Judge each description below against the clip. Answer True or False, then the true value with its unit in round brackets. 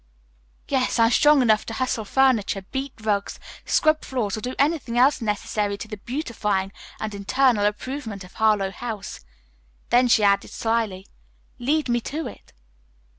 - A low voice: False (230 Hz)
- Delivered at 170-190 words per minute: False (150 wpm)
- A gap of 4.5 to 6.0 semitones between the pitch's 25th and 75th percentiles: False (4.0 semitones)